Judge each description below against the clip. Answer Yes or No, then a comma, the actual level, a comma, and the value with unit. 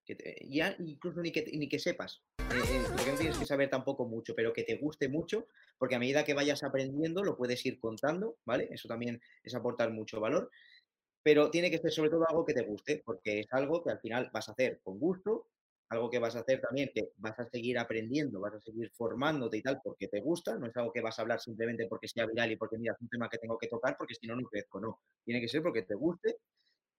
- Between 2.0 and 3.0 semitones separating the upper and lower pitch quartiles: No, average, 4.9 semitones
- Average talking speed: No, fast, 255 wpm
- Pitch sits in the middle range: No, low, 125 Hz